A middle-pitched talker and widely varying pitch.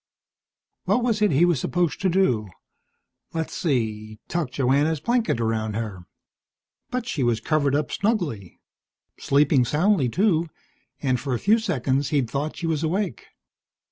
Yes: medium, 150 Hz; wide, 6.3 semitones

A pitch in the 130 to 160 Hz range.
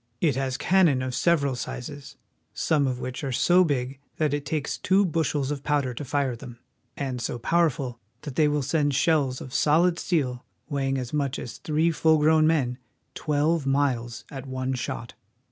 Yes: medium, 140 Hz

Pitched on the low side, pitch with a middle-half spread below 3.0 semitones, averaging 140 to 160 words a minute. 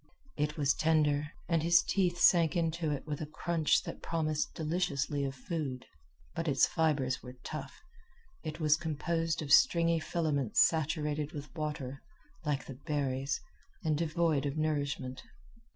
No: medium, 155 Hz; narrow, 2.5 semitones; average, 145 wpm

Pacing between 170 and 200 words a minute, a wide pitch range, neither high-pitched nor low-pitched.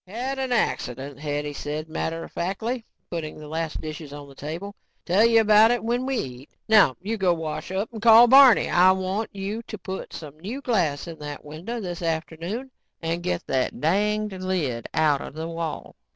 Yes: average, 190 wpm; wide, 6.0 semitones; medium, 180 Hz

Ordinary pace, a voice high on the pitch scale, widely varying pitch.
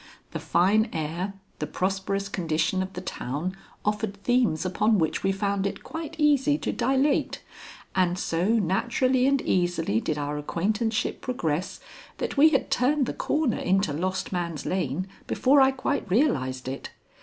Yes: average, 155 wpm; high, 195 Hz; wide, 6.5 semitones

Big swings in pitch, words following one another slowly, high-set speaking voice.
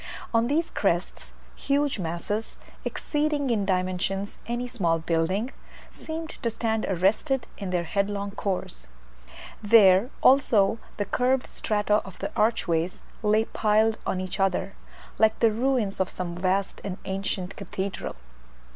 No: average, 3.7 semitones; slow, 130 wpm; high, 205 Hz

